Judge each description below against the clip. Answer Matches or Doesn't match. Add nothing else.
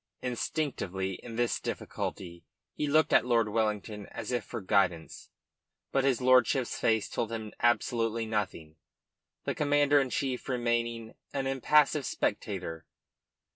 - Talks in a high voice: Doesn't match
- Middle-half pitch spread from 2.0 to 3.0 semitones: Doesn't match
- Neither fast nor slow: Doesn't match